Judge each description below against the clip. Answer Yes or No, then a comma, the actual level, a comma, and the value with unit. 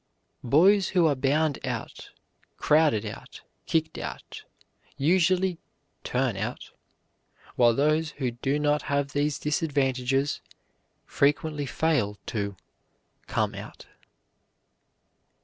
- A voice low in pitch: No, medium, 145 Hz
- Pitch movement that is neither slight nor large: Yes, average, 3.0 semitones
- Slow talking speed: Yes, slow, 95 wpm